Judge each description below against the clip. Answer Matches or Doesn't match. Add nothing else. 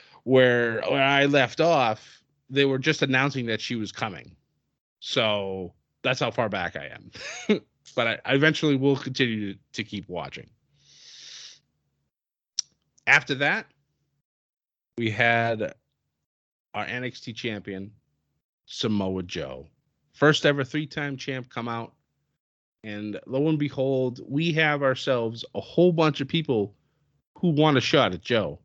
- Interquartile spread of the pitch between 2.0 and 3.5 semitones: Doesn't match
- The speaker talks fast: Doesn't match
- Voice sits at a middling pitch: Doesn't match